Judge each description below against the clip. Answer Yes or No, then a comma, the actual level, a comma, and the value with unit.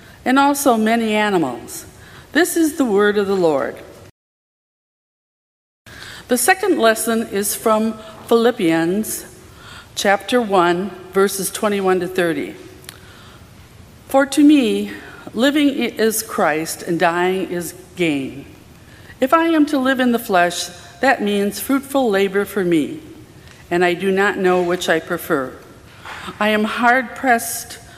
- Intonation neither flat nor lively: No, wide, 6.0 semitones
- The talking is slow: Yes, slow, 125 wpm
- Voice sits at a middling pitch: No, high, 210 Hz